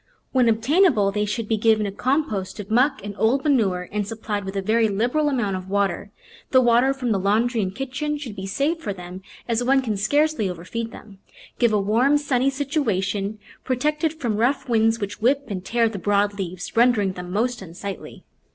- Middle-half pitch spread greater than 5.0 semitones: No, average, 4.5 semitones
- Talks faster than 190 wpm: Yes, average, 200 wpm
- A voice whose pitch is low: No, high, 225 Hz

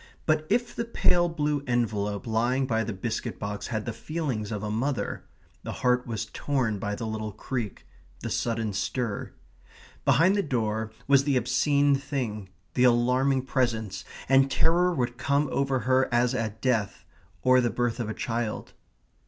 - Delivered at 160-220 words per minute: Yes, average, 165 wpm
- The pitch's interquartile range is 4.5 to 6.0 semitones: No, average, 3.8 semitones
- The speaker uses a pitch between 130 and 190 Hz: No, low, 120 Hz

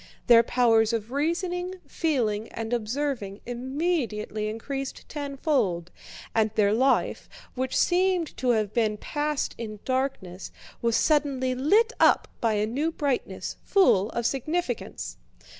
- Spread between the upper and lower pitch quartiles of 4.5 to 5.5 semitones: Yes, average, 5.1 semitones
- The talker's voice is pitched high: Yes, very high, 255 Hz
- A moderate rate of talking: No, slow, 125 wpm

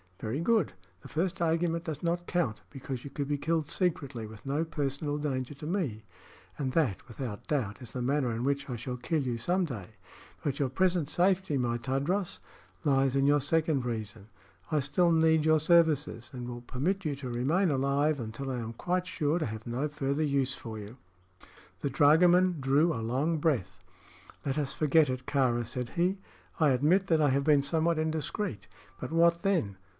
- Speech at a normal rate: Yes, average, 190 wpm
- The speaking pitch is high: No, medium, 145 Hz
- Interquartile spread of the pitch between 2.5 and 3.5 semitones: No, average, 4.5 semitones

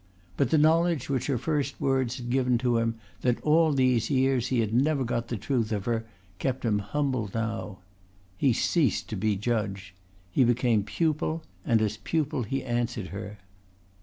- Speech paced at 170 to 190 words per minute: Yes, average, 175 wpm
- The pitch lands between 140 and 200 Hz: No, low, 120 Hz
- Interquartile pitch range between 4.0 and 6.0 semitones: No, average, 3.4 semitones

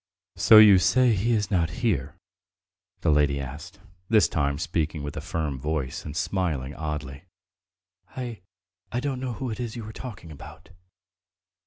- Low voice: Yes, very low, 85 Hz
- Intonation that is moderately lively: No, wide, 7.2 semitones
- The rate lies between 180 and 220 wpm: No, average, 160 wpm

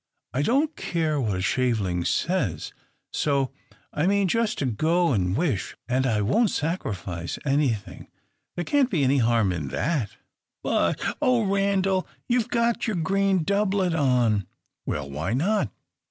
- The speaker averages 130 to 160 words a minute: Yes, average, 145 wpm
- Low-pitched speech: No, medium, 150 Hz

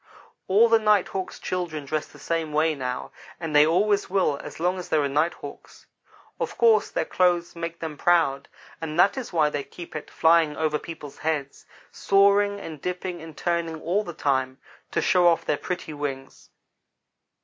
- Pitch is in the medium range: Yes, medium, 165 Hz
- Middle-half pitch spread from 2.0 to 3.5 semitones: Yes, average, 3.2 semitones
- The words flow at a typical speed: Yes, average, 180 wpm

